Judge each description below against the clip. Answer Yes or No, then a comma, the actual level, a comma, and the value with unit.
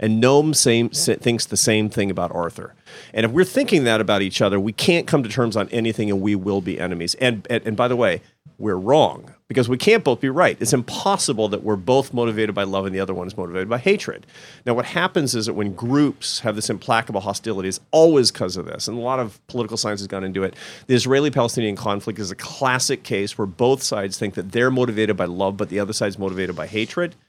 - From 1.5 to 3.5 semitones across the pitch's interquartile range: No, average, 4.3 semitones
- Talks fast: Yes, fast, 240 wpm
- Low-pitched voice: Yes, low, 115 Hz